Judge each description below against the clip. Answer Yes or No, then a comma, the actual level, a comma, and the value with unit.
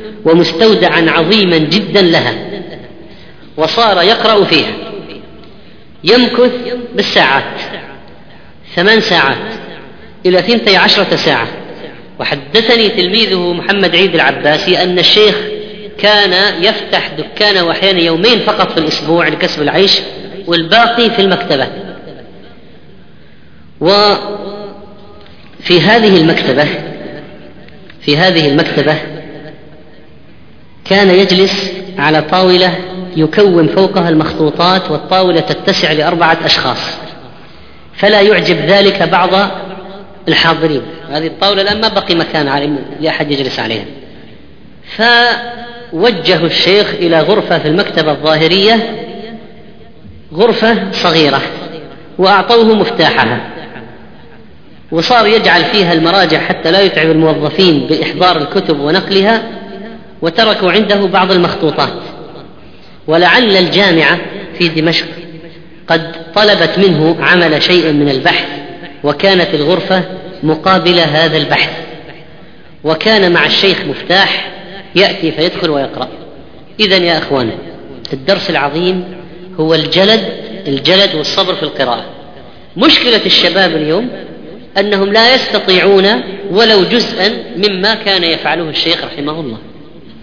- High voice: No, medium, 180 Hz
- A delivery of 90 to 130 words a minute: Yes, average, 95 wpm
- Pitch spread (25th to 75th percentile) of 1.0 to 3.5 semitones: No, average, 3.9 semitones